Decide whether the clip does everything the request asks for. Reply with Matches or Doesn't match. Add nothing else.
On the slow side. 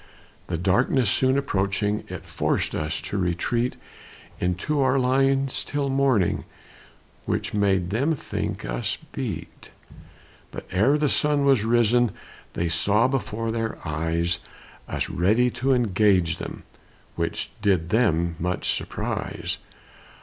Matches